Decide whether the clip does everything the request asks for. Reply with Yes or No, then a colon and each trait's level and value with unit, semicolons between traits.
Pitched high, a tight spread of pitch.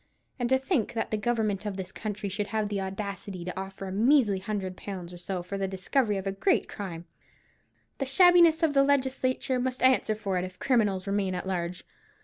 No: high, 205 Hz; average, 5.1 semitones